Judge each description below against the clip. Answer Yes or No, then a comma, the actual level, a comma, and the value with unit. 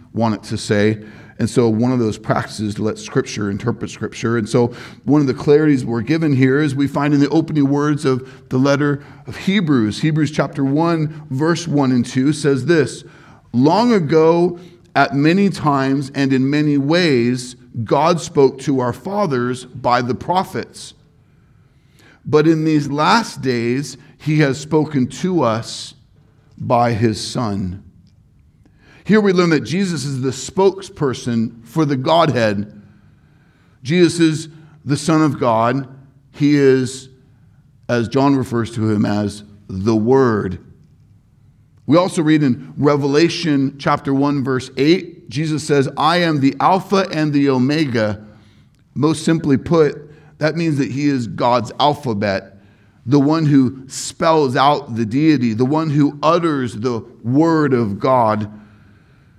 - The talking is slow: No, average, 150 wpm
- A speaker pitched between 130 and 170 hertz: Yes, low, 135 Hz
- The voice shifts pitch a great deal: No, average, 4.2 semitones